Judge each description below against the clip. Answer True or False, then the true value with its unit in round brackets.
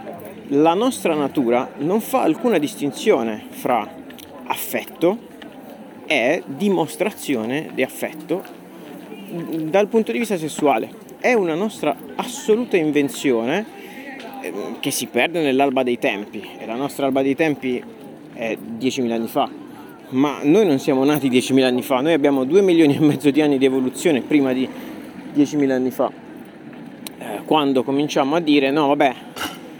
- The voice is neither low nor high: True (145 Hz)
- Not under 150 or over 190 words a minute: False (135 wpm)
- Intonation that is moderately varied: False (6.8 semitones)